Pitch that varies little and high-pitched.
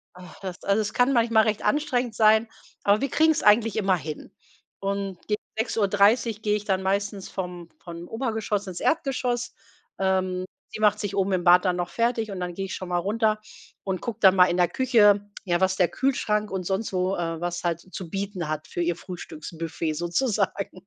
No: average, 3.3 semitones; high, 195 Hz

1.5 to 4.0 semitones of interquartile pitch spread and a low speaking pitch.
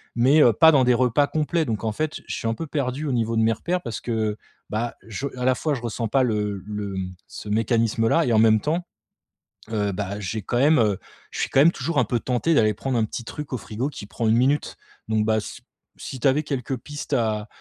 No: average, 4.4 semitones; low, 120 Hz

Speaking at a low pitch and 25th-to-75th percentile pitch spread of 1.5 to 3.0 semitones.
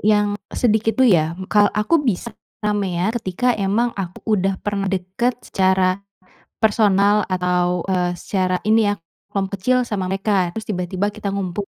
No: high, 200 Hz; narrow, 2.6 semitones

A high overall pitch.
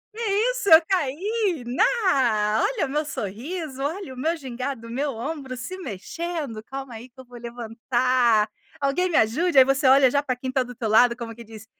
Yes: very high, 260 Hz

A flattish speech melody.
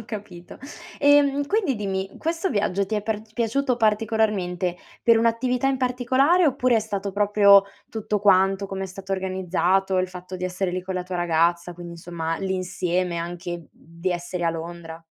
No: average, 4.0 semitones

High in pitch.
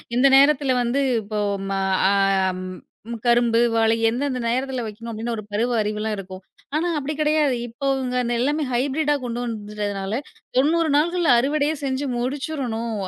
Yes: very high, 250 Hz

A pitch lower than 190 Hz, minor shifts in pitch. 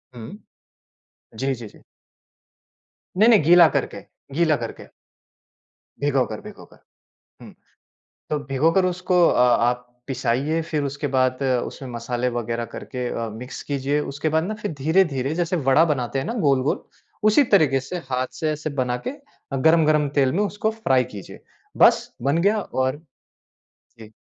No: medium, 140 Hz; average, 4.7 semitones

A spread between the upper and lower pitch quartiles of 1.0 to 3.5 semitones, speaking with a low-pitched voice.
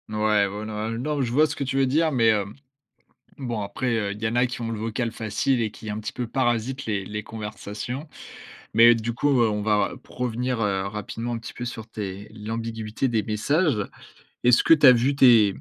Yes: average, 2.9 semitones; low, 115 Hz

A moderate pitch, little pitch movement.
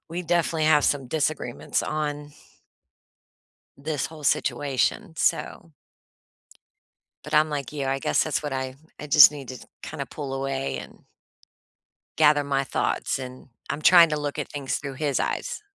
Yes: medium, 145 Hz; narrow, 2.2 semitones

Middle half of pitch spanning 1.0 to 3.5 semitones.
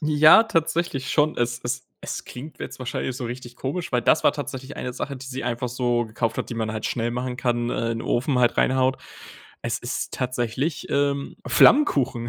Yes: average, 2.8 semitones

